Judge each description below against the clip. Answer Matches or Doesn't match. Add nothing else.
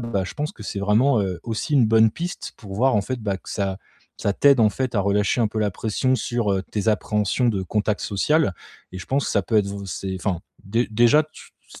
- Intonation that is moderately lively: Matches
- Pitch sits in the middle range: Doesn't match